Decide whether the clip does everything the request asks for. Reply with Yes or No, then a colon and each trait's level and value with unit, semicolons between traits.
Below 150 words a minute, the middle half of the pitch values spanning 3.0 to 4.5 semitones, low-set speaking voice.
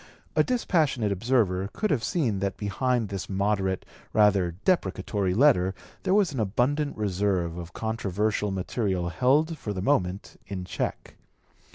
No: average, 140 wpm; average, 5.3 semitones; low, 105 Hz